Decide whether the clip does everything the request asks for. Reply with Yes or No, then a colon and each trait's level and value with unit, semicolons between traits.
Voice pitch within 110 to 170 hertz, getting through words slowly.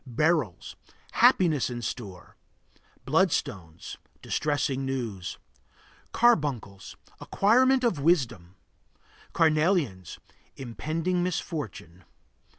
Yes: medium, 140 Hz; slow, 65 wpm